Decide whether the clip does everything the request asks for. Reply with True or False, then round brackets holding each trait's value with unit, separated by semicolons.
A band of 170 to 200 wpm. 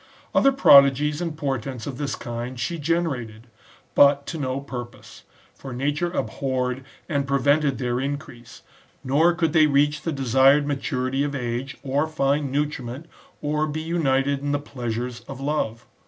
False (150 wpm)